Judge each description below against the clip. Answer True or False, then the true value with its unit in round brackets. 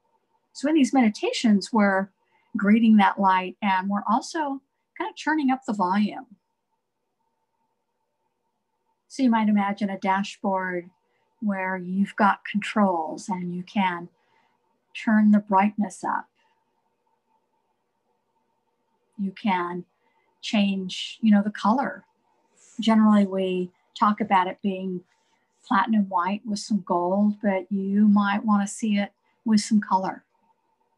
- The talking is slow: True (120 wpm)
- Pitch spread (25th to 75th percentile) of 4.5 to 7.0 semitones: True (5.3 semitones)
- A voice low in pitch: False (210 Hz)